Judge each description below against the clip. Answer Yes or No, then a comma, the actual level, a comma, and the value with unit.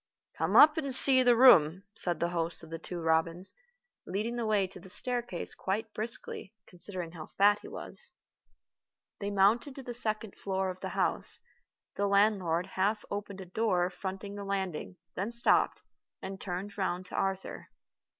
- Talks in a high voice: Yes, high, 195 Hz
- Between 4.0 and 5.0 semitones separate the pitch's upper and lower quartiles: No, average, 3.3 semitones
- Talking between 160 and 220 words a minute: Yes, average, 170 wpm